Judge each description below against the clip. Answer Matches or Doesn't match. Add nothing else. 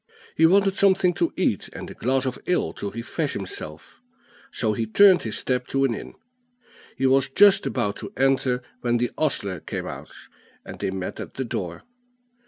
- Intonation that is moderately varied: Doesn't match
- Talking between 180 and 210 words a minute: Matches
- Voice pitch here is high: Doesn't match